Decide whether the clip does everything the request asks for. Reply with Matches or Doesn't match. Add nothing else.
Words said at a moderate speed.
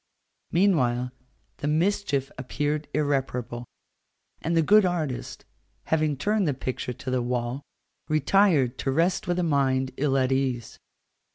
Doesn't match